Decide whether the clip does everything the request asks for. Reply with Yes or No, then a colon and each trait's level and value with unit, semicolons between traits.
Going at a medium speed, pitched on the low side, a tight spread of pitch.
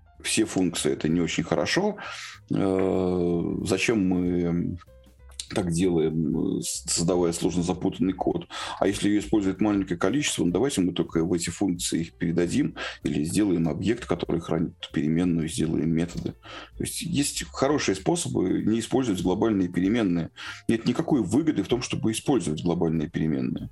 Yes: average, 140 wpm; very low, 90 Hz; narrow, 2.2 semitones